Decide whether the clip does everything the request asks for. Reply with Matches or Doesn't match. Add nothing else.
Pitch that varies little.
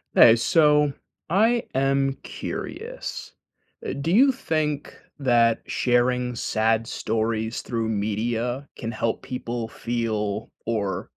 Doesn't match